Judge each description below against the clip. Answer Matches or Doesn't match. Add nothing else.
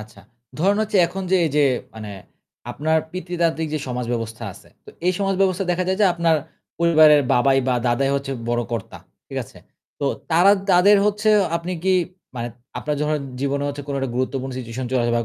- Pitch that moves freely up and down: Matches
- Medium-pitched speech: Matches